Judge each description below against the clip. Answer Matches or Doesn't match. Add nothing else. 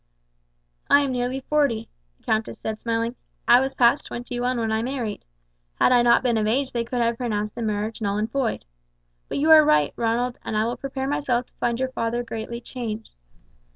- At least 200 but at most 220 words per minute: Matches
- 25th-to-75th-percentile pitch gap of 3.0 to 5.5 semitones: Doesn't match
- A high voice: Matches